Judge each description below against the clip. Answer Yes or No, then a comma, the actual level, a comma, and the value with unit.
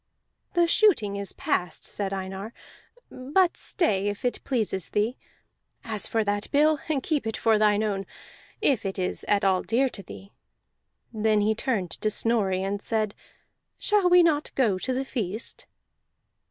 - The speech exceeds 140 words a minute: Yes, average, 155 wpm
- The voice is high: Yes, high, 215 Hz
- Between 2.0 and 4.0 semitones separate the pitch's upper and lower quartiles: No, average, 4.8 semitones